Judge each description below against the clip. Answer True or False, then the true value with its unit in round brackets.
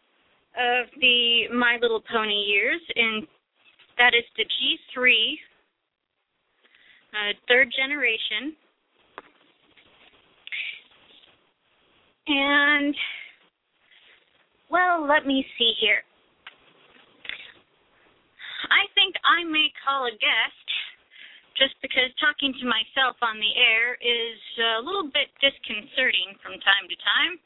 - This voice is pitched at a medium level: False (255 Hz)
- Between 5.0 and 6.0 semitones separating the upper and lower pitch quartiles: False (4.2 semitones)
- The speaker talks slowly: True (95 wpm)